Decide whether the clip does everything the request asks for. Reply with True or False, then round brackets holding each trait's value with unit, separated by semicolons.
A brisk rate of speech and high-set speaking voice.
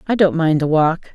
False (260 wpm; 165 Hz)